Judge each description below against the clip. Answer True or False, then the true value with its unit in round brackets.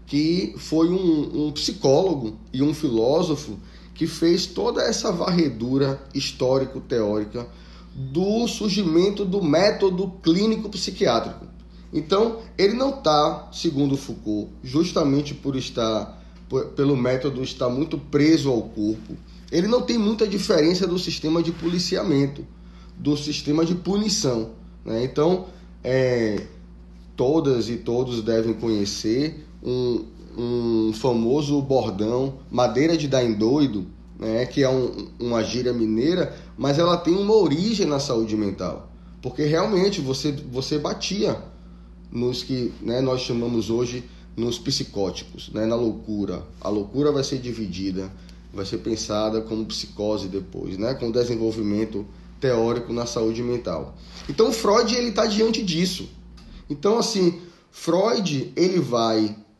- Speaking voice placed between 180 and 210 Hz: False (135 Hz)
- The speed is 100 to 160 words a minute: True (125 wpm)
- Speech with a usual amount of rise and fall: False (7.3 semitones)